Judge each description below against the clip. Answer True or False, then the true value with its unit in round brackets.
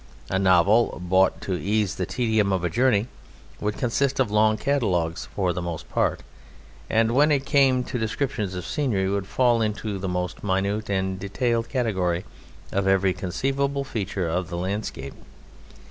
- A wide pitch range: False (4.2 semitones)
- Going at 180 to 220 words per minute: False (160 wpm)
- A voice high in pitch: False (100 Hz)